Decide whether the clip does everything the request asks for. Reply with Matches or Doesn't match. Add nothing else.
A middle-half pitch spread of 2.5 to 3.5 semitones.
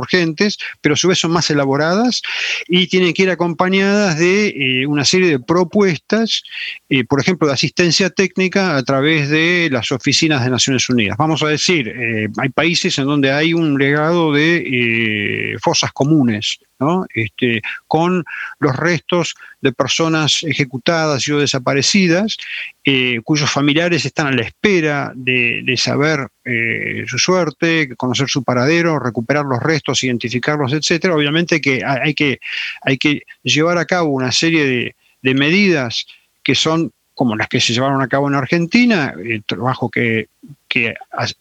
Doesn't match